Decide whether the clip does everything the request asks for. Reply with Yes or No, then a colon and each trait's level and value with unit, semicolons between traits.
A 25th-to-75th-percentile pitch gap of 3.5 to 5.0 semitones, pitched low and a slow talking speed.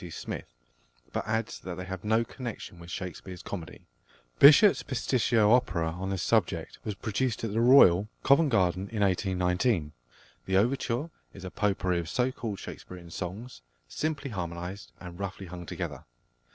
No: average, 4.5 semitones; very low, 95 Hz; average, 155 wpm